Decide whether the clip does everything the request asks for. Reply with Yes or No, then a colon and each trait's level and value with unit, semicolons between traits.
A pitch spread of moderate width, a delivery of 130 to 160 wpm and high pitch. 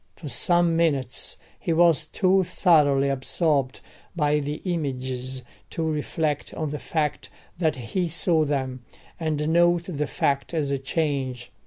No: average, 3.4 semitones; average, 140 wpm; medium, 150 Hz